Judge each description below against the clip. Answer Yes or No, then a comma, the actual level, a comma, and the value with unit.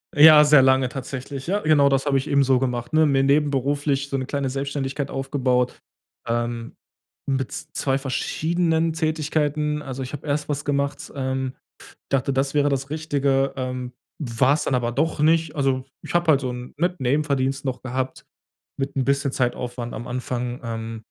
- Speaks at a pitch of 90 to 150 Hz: Yes, low, 135 Hz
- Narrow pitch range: Yes, narrow, 2.2 semitones